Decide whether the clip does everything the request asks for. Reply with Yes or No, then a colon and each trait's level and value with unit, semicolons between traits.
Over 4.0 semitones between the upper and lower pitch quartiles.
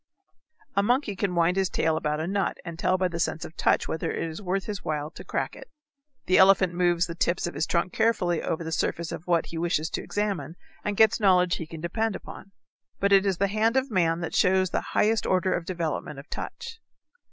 No: average, 3.0 semitones